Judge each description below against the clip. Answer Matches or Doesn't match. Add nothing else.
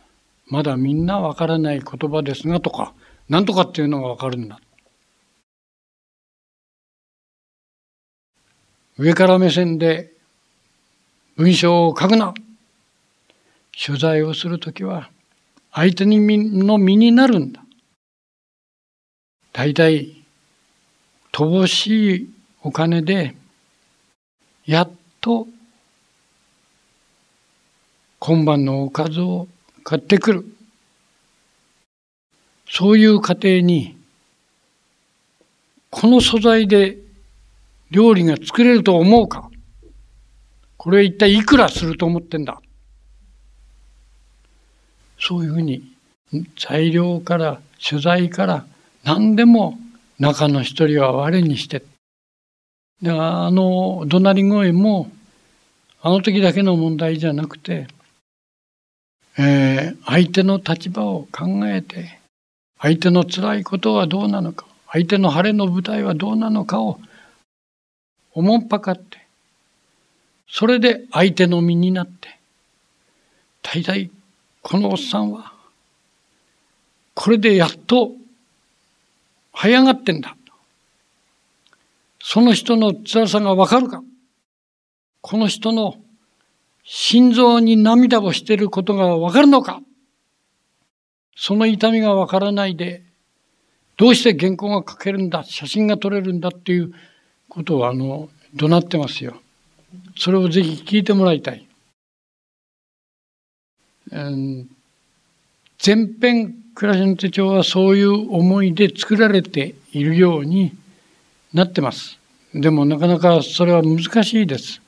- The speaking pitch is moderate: Matches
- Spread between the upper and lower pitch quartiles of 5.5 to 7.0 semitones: Doesn't match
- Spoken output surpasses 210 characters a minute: Doesn't match